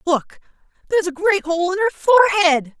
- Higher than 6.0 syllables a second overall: Yes, 7.8 syllables/s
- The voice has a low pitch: No, very high, 360 Hz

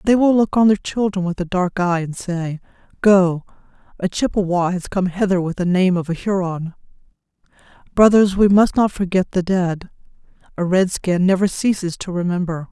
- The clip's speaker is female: Yes, female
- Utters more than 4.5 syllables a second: Yes, 5.0 syllables/s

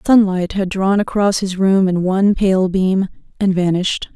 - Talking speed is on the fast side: No, average, 175 wpm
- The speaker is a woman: Yes, female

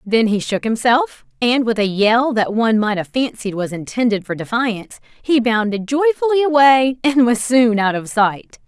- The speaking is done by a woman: Yes, female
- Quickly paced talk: No, average, 185 wpm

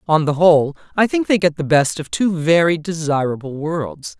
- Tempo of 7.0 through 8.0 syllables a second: No, 5.0 syllables/s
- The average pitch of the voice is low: No, medium, 160 Hz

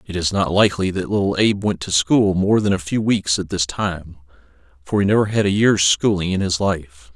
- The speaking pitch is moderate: No, very low, 95 Hz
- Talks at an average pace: No, fast, 235 wpm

